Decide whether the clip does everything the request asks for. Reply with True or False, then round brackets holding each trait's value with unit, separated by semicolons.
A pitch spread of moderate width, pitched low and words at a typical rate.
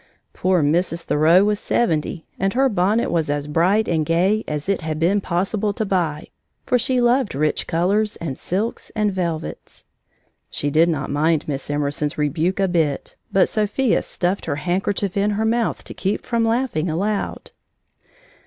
False (5.0 semitones; 180 Hz; 165 wpm)